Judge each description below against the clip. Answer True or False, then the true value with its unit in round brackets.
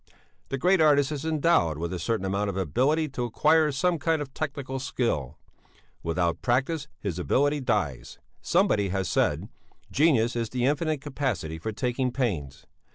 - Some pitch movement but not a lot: False (7.4 semitones)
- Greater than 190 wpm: False (160 wpm)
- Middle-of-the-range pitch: False (130 Hz)